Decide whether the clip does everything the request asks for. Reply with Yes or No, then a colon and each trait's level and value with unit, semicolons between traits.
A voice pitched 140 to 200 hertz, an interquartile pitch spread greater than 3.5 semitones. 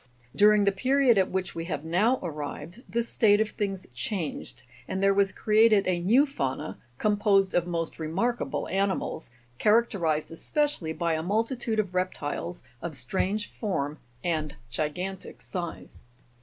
Yes: high, 190 Hz; average, 4.4 semitones